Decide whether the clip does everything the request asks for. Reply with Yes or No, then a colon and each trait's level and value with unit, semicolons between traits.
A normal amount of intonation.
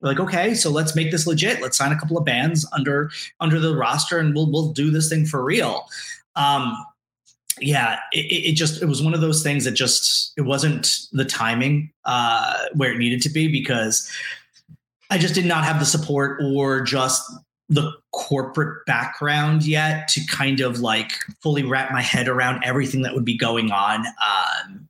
Yes: average, 3.3 semitones